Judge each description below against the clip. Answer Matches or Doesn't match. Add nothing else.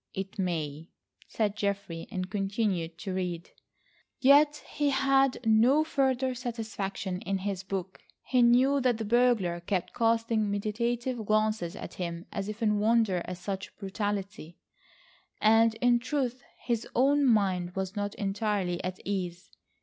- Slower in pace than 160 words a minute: Matches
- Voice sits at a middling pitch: Doesn't match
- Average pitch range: Matches